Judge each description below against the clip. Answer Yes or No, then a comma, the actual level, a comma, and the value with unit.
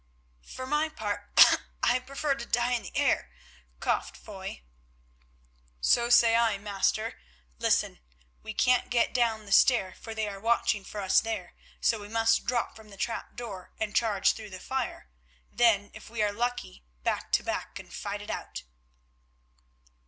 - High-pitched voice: Yes, high, 225 Hz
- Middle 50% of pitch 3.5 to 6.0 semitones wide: No, average, 2.8 semitones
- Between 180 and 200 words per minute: No, average, 165 wpm